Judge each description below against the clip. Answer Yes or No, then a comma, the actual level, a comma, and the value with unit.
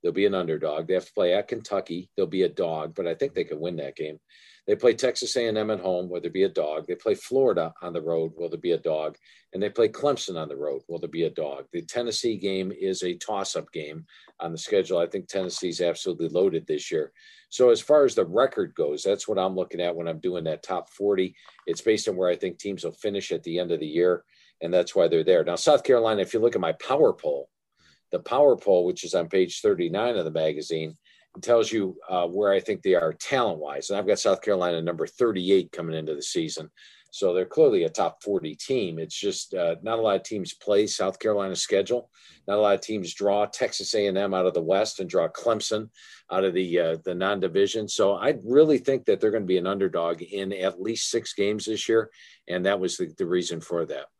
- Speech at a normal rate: No, fast, 240 wpm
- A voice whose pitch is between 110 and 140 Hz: Yes, low, 135 Hz